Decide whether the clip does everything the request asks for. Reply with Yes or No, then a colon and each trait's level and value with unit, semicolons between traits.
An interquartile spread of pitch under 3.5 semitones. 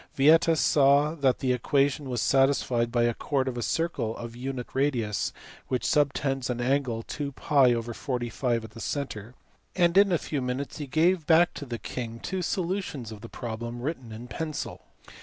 No: average, 3.8 semitones